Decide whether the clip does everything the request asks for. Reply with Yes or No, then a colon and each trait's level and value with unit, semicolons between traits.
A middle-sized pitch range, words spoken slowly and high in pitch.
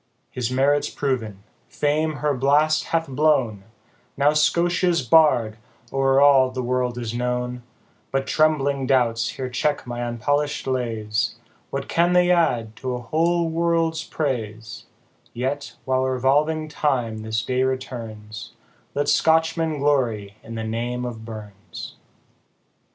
No: average, 4.2 semitones; slow, 130 wpm; low, 130 Hz